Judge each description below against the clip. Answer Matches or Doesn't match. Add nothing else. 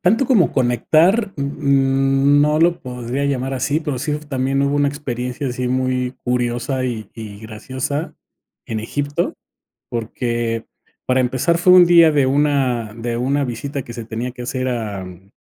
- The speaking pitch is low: Matches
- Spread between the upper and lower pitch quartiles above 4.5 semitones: Doesn't match